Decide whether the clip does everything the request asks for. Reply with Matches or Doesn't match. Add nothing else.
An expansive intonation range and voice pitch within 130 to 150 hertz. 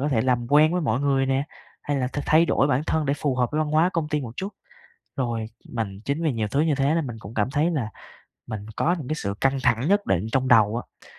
Doesn't match